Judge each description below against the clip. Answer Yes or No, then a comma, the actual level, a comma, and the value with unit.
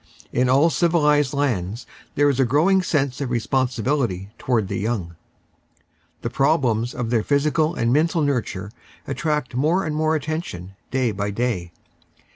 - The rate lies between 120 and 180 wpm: Yes, average, 145 wpm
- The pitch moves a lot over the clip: No, average, 4.7 semitones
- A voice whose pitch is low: Yes, low, 130 Hz